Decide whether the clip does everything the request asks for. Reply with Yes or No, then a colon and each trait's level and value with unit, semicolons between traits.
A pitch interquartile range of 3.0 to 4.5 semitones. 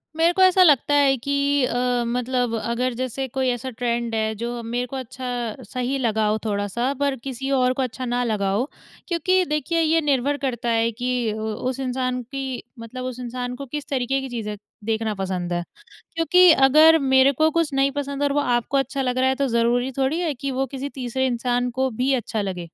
No: narrow, 2.6 semitones